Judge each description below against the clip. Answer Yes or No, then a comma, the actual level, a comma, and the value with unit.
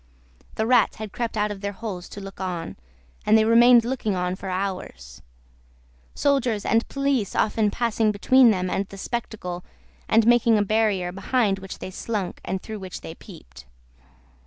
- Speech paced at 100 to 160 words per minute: No, average, 170 wpm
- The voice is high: Yes, high, 210 Hz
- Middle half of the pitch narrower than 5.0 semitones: Yes, average, 3.4 semitones